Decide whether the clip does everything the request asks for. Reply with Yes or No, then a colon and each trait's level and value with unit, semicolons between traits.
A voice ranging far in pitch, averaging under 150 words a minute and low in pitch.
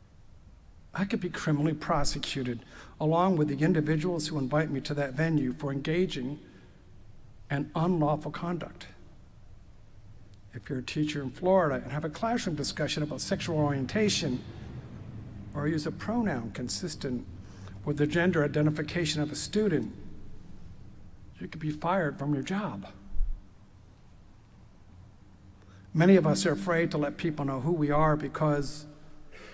No: wide, 7.5 semitones; slow, 135 wpm; medium, 145 Hz